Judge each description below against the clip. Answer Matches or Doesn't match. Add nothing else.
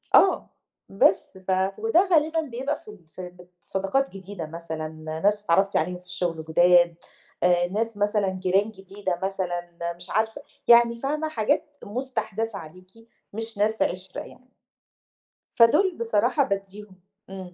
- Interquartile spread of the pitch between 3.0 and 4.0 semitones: Doesn't match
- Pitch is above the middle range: Matches